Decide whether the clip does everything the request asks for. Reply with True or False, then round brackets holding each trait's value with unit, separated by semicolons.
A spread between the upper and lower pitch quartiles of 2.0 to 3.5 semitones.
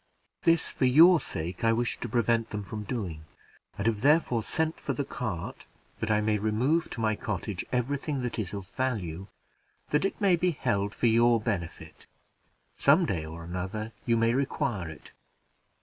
False (4.7 semitones)